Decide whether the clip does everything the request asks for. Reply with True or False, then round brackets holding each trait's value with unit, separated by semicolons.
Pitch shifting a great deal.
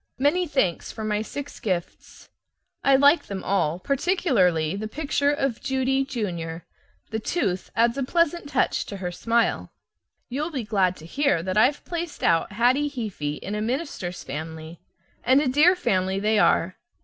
True (7.3 semitones)